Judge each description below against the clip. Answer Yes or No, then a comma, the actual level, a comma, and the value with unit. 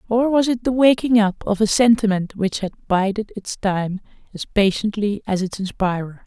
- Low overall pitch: No, high, 210 Hz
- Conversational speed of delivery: Yes, average, 180 wpm